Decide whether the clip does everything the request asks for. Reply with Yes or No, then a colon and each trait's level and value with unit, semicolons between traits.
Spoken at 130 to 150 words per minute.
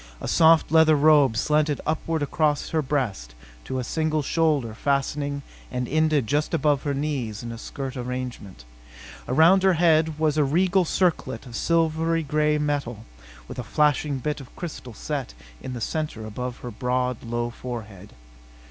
No: average, 160 wpm